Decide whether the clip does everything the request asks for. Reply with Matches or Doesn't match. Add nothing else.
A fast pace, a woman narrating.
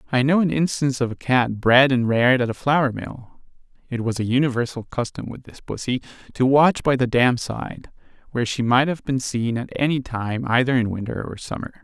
Doesn't match